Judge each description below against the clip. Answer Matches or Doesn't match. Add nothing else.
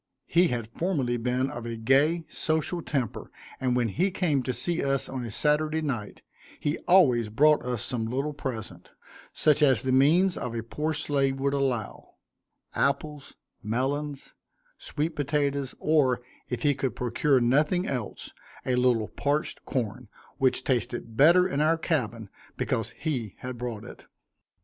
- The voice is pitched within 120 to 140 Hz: Matches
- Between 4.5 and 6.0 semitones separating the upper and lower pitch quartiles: Doesn't match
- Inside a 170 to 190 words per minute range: Doesn't match